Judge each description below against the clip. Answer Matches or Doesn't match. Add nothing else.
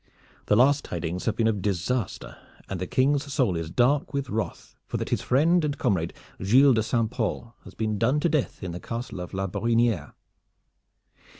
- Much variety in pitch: Matches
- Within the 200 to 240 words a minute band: Doesn't match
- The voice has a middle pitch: Doesn't match